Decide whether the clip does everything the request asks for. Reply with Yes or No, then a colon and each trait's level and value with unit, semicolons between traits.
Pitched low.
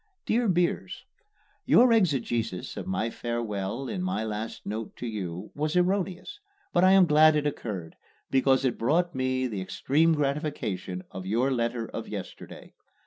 Yes: low, 130 Hz